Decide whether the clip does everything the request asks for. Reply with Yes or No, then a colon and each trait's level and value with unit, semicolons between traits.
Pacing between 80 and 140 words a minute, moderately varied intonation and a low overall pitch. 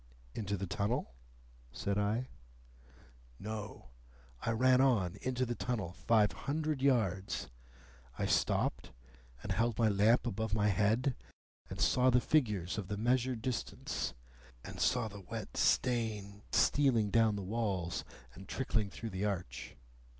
Yes: slow, 135 wpm; average, 3.7 semitones; low, 110 Hz